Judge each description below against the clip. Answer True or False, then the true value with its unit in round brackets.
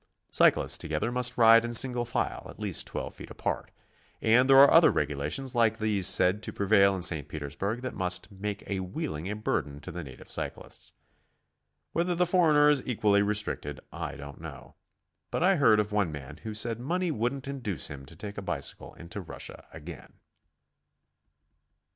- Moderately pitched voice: False (105 Hz)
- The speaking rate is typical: True (170 wpm)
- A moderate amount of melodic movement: False (5.8 semitones)